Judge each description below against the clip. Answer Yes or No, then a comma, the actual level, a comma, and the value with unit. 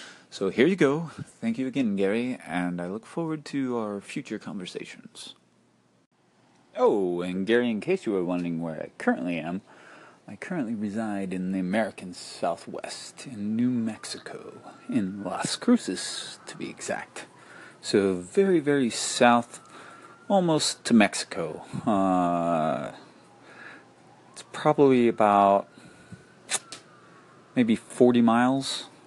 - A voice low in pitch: Yes, low, 115 Hz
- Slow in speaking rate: Yes, slow, 120 wpm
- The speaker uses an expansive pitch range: Yes, wide, 7.2 semitones